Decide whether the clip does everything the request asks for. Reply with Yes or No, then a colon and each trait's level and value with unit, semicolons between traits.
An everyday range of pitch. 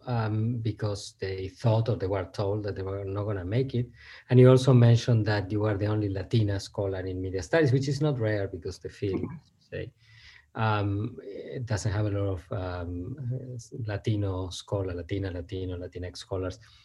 Yes: average, 3.6 semitones